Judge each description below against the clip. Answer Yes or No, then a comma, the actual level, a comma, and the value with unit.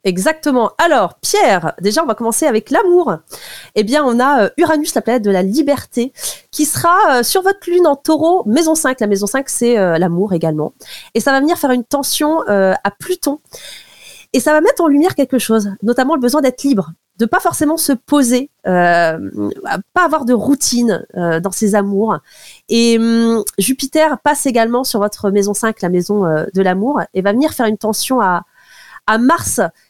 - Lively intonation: Yes, wide, 6.5 semitones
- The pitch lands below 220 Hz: No, high, 245 Hz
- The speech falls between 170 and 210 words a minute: Yes, average, 185 wpm